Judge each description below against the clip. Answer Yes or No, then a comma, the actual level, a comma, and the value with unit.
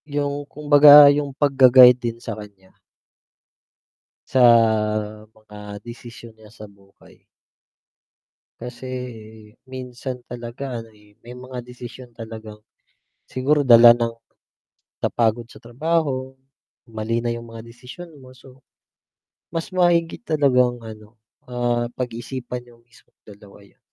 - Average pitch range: No, narrow, 2.2 semitones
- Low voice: Yes, low, 120 Hz